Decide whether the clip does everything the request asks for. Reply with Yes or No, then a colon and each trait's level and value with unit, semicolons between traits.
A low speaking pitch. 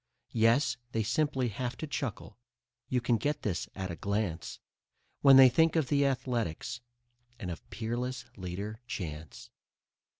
Yes: low, 120 Hz